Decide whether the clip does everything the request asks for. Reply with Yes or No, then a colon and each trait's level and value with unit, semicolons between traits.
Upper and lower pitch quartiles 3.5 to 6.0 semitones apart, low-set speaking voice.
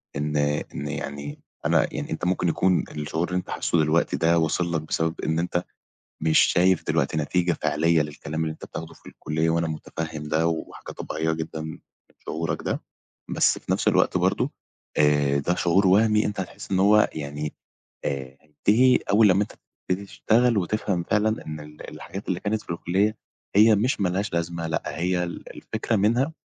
Yes: average, 3.8 semitones; very low, 85 Hz